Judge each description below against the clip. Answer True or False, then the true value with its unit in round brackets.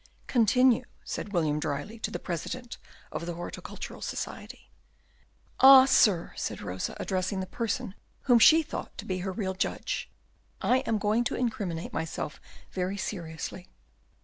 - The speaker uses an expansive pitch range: True (5.7 semitones)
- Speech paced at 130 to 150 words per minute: True (145 wpm)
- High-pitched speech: True (200 Hz)